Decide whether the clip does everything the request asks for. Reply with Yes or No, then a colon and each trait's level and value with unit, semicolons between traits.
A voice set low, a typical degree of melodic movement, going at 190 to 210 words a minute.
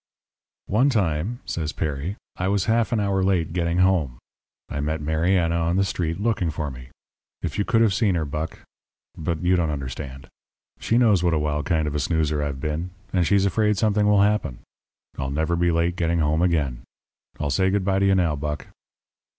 Yes: very low, 85 Hz; average, 4.2 semitones; average, 200 wpm